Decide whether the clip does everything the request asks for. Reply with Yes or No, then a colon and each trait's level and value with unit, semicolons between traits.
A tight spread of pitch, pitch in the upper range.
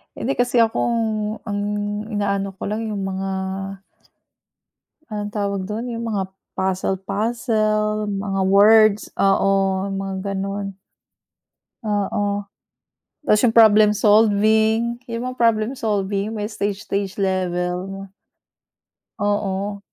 Yes: narrow, 1.9 semitones; high, 205 Hz